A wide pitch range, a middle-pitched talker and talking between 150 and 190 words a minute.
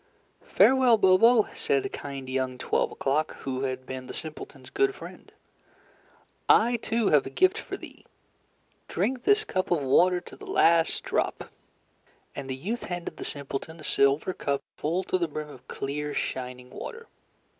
Yes: wide, 8.6 semitones; medium, 155 Hz; average, 160 wpm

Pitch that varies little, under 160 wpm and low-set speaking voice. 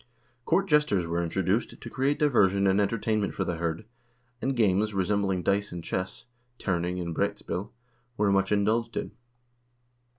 No: average, 3.2 semitones; average, 145 wpm; low, 100 Hz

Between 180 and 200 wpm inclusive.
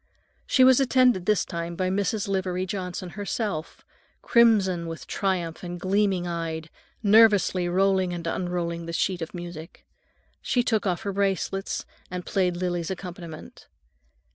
No: average, 140 wpm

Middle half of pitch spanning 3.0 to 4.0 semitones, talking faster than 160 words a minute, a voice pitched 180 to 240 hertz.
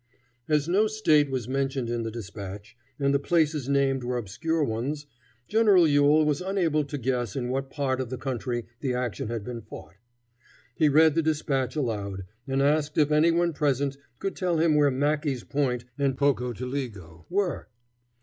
No: average, 3.7 semitones; average, 170 wpm; medium, 140 Hz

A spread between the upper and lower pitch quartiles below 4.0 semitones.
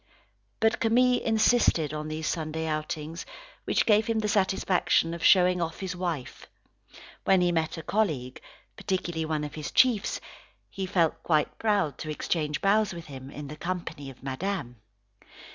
No: average, 4.4 semitones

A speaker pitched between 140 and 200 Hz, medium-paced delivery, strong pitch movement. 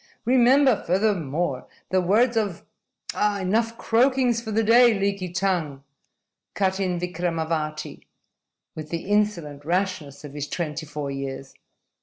No: medium, 185 Hz; slow, 125 wpm; wide, 5.9 semitones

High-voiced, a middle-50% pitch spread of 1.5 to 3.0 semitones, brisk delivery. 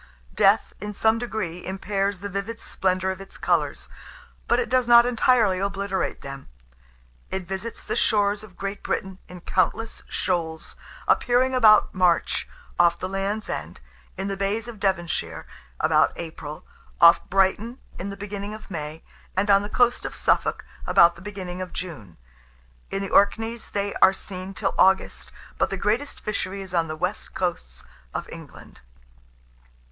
No: high, 195 Hz; narrow, 2.6 semitones; average, 160 wpm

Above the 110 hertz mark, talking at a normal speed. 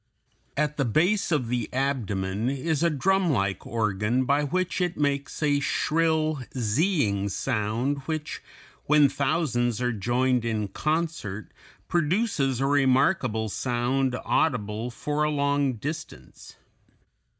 No: low, 135 Hz; slow, 115 wpm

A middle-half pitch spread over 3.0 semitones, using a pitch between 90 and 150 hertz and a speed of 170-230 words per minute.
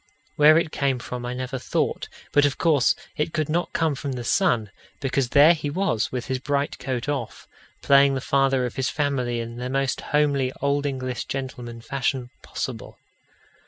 No: narrow, 2.5 semitones; low, 135 Hz; average, 180 wpm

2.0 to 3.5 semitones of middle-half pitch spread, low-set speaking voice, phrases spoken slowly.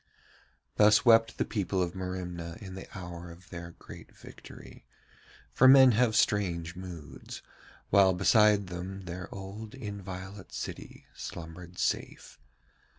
Yes: average, 3.0 semitones; very low, 95 Hz; slow, 125 wpm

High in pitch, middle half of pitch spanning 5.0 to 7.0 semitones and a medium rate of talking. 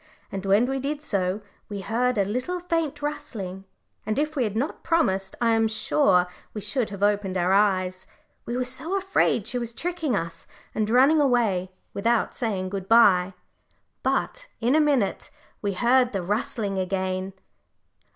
Yes: high, 220 Hz; wide, 5.5 semitones; average, 165 wpm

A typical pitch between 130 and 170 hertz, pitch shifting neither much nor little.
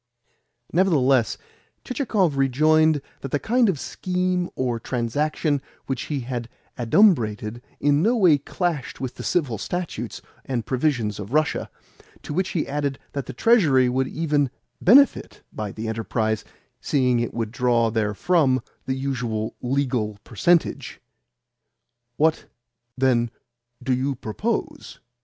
Yes: low, 135 Hz; average, 4.8 semitones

